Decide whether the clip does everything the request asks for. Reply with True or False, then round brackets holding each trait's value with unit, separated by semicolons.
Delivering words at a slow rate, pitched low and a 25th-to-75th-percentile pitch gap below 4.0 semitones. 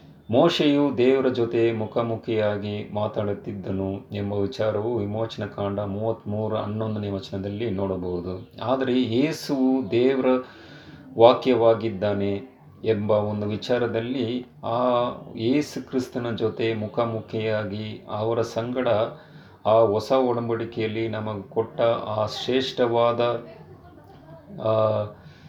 False (80 wpm; 115 Hz; 2.8 semitones)